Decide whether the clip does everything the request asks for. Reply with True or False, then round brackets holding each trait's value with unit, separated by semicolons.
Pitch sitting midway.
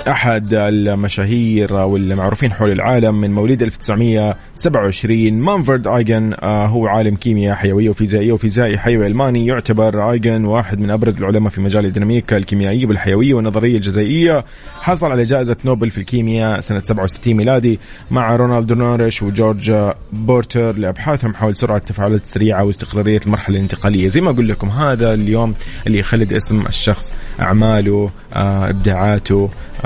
False (110 Hz)